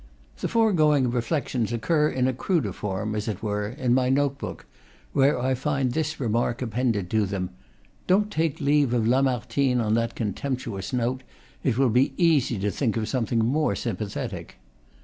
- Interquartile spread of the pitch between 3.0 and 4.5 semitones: Yes, average, 3.9 semitones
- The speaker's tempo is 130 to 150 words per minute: No, average, 170 wpm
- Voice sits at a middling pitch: No, low, 125 Hz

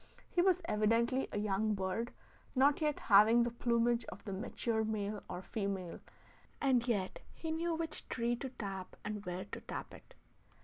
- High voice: Yes, high, 225 Hz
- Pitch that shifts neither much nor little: Yes, average, 4.1 semitones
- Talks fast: No, average, 170 wpm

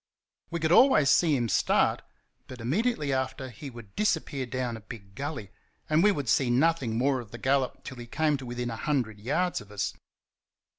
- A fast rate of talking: No, average, 195 wpm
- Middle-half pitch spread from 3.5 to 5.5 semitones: Yes, average, 4.4 semitones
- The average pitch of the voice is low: Yes, low, 130 Hz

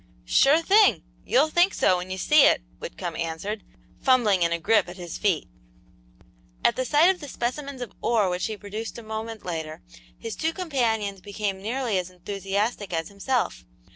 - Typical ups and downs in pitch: No, wide, 5.7 semitones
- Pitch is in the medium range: No, high, 215 Hz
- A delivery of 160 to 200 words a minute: Yes, average, 170 wpm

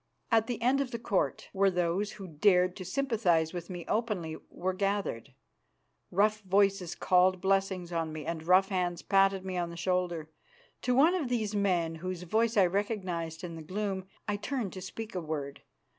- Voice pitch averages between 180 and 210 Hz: Yes, medium, 185 Hz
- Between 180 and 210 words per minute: Yes, average, 185 wpm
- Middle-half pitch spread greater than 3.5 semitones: No, average, 3.2 semitones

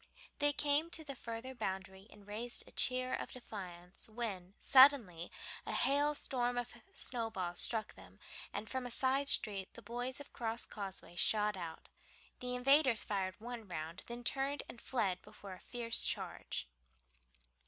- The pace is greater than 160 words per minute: No, average, 155 wpm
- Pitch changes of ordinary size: Yes, average, 5.0 semitones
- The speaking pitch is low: No, high, 230 Hz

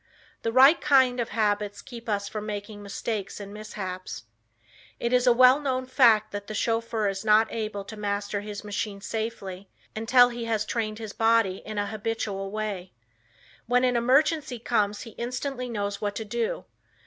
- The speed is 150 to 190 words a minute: Yes, average, 170 wpm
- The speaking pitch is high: Yes, high, 220 Hz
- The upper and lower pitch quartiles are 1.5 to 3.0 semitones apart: Yes, average, 2.7 semitones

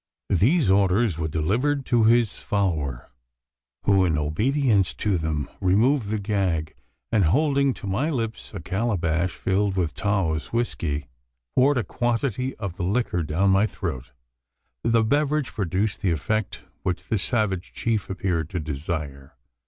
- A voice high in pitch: No, low, 100 Hz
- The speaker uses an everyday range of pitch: No, wide, 5.8 semitones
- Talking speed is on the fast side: No, average, 145 wpm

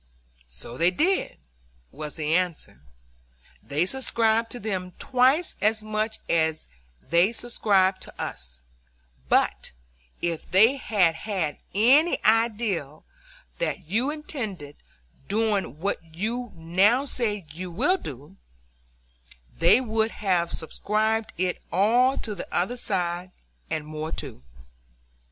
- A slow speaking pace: Yes, slow, 115 wpm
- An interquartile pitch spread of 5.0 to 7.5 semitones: Yes, wide, 5.4 semitones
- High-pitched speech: Yes, high, 195 Hz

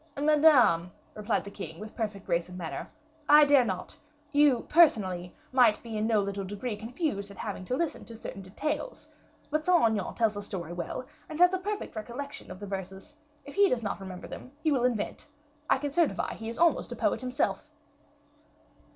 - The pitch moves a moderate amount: No, wide, 6.6 semitones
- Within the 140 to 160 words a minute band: No, average, 195 wpm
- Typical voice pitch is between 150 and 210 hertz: No, high, 225 Hz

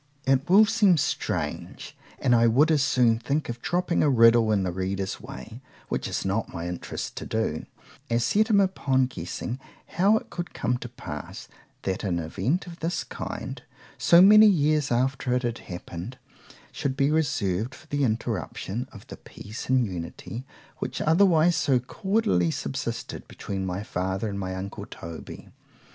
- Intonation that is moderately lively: No, wide, 7.8 semitones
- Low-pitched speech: Yes, low, 125 Hz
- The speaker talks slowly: No, average, 165 wpm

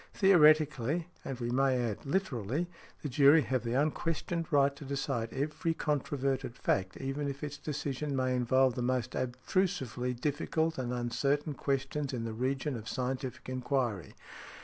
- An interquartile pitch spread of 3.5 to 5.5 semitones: No, average, 3.0 semitones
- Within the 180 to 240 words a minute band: No, average, 150 wpm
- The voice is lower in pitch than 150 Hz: Yes, low, 135 Hz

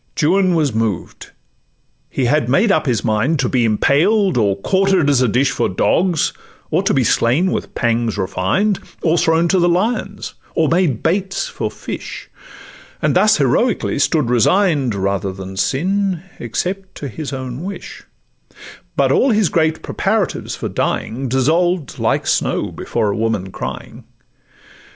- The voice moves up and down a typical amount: No, wide, 7.9 semitones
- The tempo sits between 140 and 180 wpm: Yes, average, 145 wpm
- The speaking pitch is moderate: Yes, medium, 150 Hz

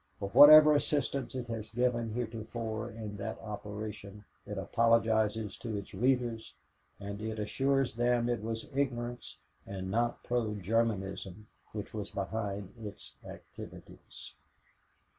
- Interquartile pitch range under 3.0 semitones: Yes, narrow, 2.6 semitones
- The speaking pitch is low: Yes, low, 110 Hz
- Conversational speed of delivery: No, slow, 120 wpm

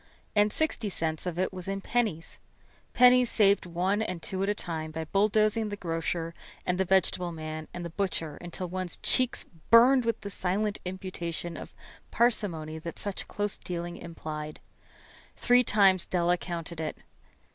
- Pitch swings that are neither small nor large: Yes, average, 3.6 semitones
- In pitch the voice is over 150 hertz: Yes, medium, 185 Hz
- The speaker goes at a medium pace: Yes, average, 160 wpm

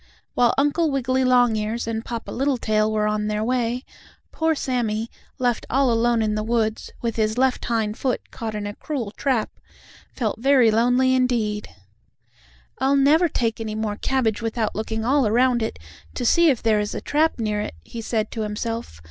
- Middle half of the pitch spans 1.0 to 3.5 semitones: Yes, average, 3.0 semitones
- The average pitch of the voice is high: Yes, high, 230 Hz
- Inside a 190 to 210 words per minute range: No, average, 180 wpm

